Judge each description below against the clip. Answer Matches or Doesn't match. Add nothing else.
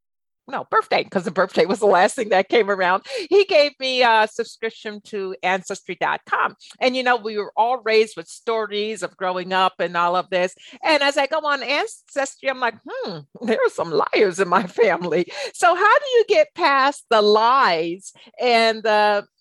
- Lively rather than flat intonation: Matches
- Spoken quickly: Doesn't match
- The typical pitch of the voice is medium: Doesn't match